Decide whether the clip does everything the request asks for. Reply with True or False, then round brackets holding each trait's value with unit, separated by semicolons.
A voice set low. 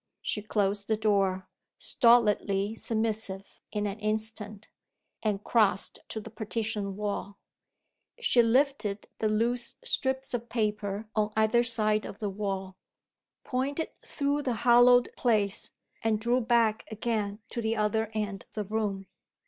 False (215 Hz)